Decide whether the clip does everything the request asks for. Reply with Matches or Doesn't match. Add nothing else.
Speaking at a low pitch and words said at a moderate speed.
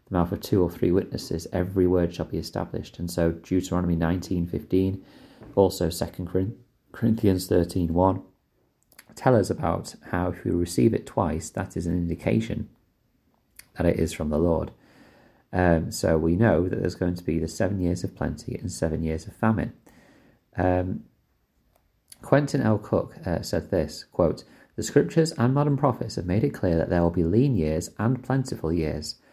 Matches